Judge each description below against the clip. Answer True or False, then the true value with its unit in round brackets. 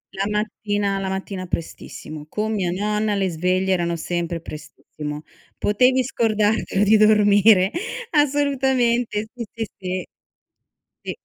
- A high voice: True (205 Hz)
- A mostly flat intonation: False (3.2 semitones)